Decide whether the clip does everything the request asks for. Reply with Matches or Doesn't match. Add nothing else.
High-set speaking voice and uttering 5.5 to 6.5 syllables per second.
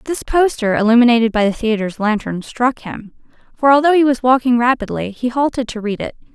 Matches